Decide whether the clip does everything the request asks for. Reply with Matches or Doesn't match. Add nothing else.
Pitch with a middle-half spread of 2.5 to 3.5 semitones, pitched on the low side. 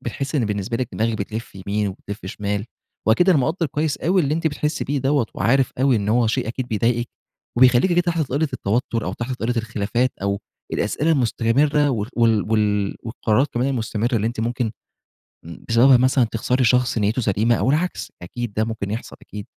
Doesn't match